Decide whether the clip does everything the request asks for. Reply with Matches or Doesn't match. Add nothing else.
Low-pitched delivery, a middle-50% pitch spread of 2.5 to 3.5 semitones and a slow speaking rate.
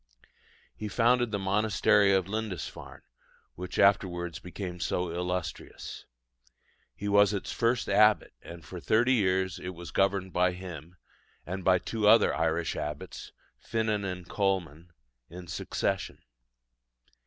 Matches